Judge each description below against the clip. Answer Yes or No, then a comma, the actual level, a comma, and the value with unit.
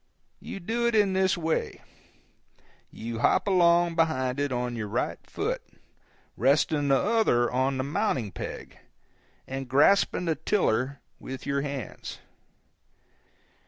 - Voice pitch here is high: No, medium, 140 Hz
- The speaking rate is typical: No, slow, 125 wpm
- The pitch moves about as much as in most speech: No, wide, 5.7 semitones